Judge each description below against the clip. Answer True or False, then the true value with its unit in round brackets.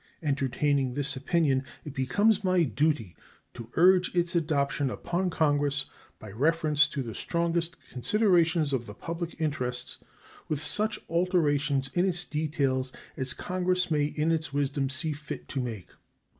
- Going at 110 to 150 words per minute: True (145 wpm)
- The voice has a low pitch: False (150 Hz)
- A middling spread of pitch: True (4.0 semitones)